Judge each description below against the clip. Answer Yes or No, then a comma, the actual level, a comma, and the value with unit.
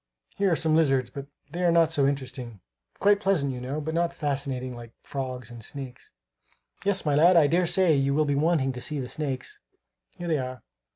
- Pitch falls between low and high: Yes, medium, 145 Hz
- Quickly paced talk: Yes, fast, 210 wpm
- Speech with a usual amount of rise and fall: Yes, average, 4.3 semitones